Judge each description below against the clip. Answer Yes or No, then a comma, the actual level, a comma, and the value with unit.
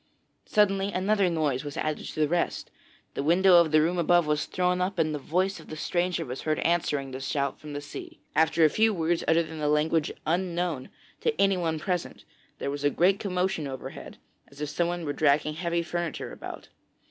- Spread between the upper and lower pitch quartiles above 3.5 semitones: No, average, 3.1 semitones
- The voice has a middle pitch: Yes, medium, 165 Hz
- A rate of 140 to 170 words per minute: No, average, 200 wpm